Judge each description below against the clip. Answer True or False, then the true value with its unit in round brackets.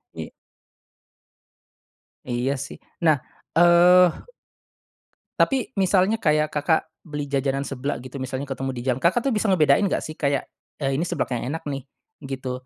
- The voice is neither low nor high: True (145 Hz)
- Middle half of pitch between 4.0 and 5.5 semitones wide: True (4.4 semitones)